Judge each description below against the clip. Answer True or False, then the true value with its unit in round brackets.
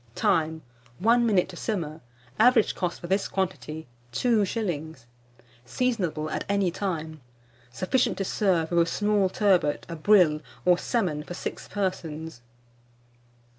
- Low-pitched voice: False (180 Hz)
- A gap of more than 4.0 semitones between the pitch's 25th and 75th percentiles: True (4.4 semitones)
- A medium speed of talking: False (130 wpm)